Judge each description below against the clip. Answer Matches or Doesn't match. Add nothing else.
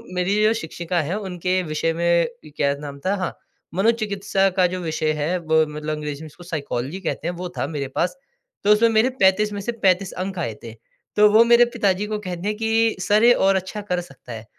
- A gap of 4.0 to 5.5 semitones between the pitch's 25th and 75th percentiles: Matches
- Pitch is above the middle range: Doesn't match